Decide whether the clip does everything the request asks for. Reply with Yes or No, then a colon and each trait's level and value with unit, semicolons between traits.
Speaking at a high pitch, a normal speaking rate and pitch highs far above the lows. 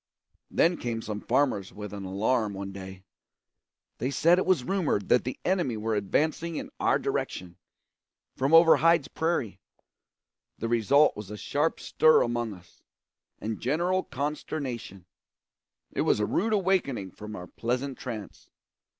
No: low, 120 Hz; average, 145 wpm; wide, 7.2 semitones